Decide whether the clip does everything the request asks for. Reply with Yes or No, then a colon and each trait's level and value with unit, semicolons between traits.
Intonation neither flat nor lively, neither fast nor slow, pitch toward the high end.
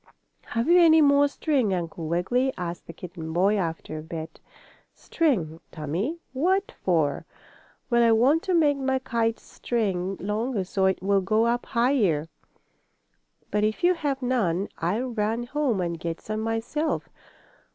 No: wide, 7.0 semitones; average, 150 wpm; high, 220 Hz